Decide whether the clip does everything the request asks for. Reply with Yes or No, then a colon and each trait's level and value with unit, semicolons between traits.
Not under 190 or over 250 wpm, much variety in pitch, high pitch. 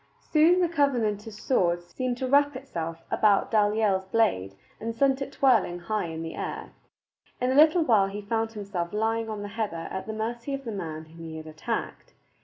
Yes: average, 195 wpm; wide, 6.3 semitones; high, 215 Hz